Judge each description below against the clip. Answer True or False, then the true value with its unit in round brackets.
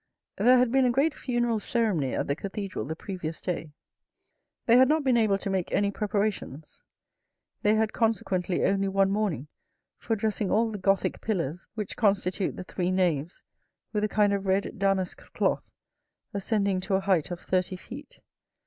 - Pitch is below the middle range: False (200 Hz)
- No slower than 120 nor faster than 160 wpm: False (170 wpm)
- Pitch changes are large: False (3.0 semitones)